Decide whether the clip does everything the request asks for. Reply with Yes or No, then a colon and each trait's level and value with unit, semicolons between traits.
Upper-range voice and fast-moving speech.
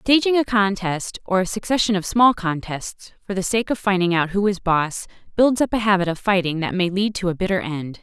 Yes: high, 195 Hz; fast, 230 wpm